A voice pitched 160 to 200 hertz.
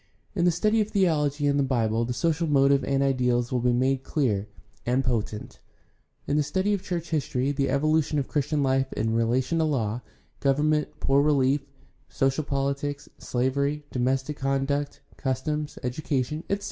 No: medium, 140 Hz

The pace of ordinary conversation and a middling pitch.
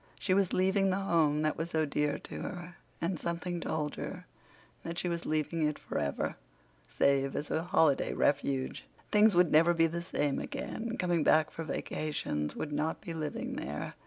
Yes: average, 180 wpm; medium, 165 Hz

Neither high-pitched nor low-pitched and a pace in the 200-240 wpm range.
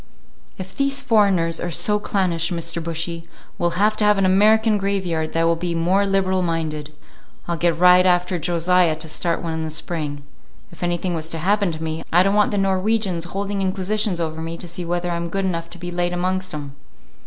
Yes: medium, 175 Hz; fast, 205 wpm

